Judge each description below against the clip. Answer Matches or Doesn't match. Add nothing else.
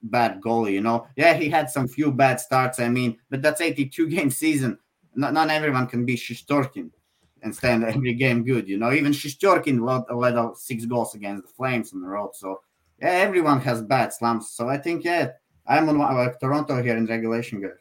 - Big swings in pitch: Doesn't match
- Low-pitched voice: Matches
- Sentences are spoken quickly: Matches